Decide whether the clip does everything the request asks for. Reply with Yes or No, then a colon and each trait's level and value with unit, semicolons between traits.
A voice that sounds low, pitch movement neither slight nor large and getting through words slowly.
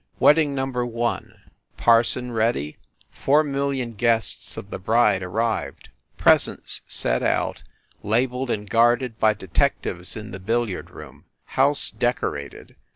Yes: low, 115 Hz; average, 3.2 semitones; slow, 130 wpm